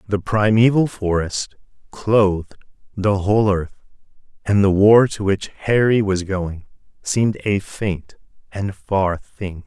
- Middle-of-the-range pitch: No, low, 100 Hz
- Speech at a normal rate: No, slow, 130 wpm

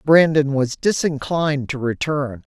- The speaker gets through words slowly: Yes, slow, 120 wpm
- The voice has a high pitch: No, medium, 145 Hz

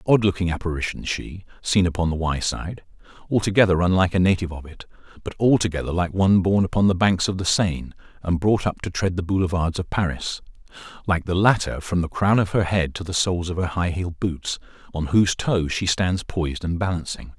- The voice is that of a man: Yes, male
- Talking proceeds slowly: No, average, 200 wpm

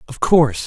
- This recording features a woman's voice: No, male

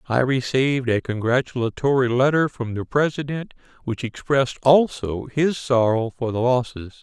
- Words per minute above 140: No, slow, 135 wpm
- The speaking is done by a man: Yes, male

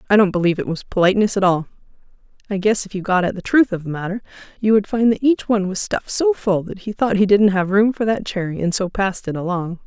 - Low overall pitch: No, high, 200 Hz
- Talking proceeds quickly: Yes, fast, 270 wpm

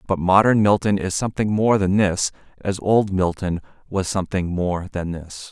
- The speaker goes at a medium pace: Yes, average, 175 wpm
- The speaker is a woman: No, male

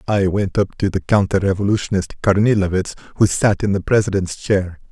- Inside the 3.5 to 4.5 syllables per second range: No, 5.5 syllables/s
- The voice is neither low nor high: No, very low, 95 Hz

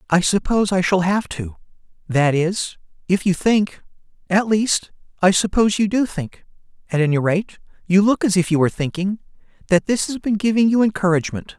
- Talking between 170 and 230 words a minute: No, average, 160 wpm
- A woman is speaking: No, male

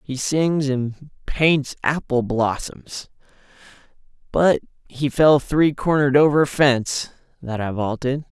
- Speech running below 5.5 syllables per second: Yes, 3.9 syllables/s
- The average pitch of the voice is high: No, low, 135 Hz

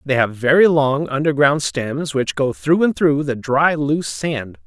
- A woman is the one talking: No, male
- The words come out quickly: No, average, 195 wpm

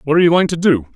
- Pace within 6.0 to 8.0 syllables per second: No, 8.9 syllables/s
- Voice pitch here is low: No, medium, 155 Hz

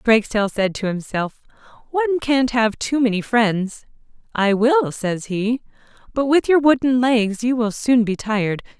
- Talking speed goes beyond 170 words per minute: No, average, 165 wpm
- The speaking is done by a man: No, female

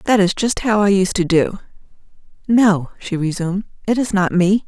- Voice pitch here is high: Yes, high, 195 Hz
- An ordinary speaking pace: Yes, average, 180 wpm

